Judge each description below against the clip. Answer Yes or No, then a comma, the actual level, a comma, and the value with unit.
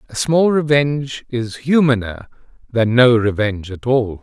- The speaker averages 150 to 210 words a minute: No, average, 140 wpm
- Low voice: Yes, low, 125 Hz